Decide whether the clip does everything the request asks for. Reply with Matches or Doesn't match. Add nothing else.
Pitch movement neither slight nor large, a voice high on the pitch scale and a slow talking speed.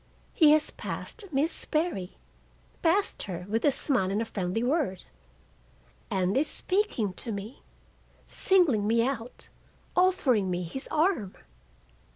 Doesn't match